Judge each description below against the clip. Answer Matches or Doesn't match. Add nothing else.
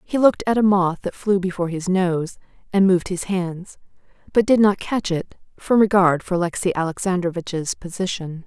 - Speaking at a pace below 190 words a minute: Matches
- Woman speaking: Matches